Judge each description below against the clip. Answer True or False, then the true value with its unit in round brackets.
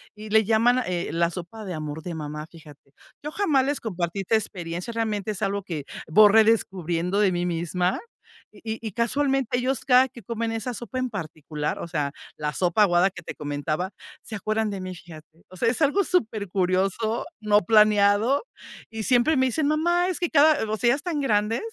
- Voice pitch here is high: True (210 Hz)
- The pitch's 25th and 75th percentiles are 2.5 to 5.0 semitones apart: False (5.5 semitones)